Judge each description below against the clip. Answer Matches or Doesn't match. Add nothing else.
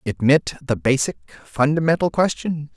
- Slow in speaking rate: Matches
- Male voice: Matches